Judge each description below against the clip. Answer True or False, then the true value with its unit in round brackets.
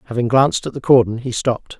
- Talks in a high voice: False (125 Hz)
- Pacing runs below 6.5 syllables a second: False (6.9 syllables/s)